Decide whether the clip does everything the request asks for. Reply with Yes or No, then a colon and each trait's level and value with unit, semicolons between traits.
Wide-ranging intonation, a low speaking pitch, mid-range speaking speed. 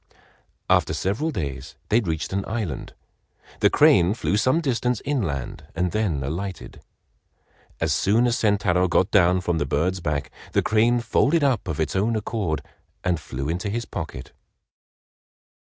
Yes: wide, 5.9 semitones; very low, 95 Hz; average, 150 wpm